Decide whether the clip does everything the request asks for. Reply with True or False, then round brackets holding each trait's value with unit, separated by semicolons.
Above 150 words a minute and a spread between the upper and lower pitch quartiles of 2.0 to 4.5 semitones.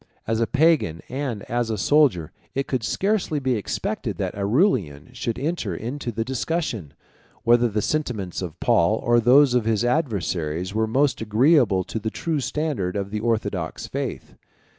False (160 wpm; 5.4 semitones)